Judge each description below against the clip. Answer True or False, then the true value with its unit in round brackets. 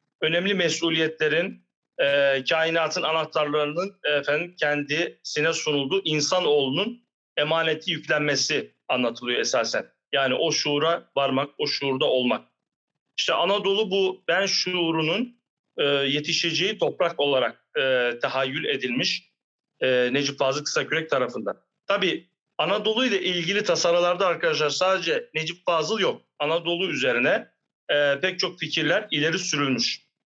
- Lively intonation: False (3.7 semitones)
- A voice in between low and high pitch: True (160 Hz)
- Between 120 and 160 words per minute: False (105 wpm)